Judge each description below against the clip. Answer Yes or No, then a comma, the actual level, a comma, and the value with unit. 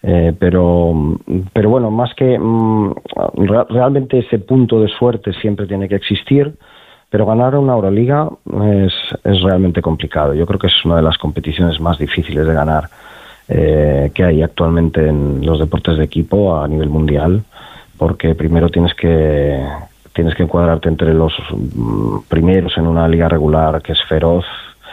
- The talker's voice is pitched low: Yes, very low, 85 Hz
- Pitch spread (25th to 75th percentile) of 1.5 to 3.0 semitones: No, average, 4.2 semitones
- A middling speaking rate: Yes, average, 155 wpm